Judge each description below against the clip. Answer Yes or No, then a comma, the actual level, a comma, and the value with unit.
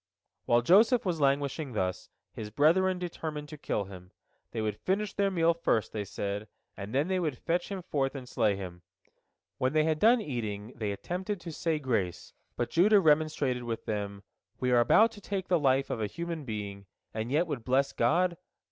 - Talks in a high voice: No, medium, 140 Hz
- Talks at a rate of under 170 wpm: No, average, 190 wpm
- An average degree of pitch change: No, wide, 7.8 semitones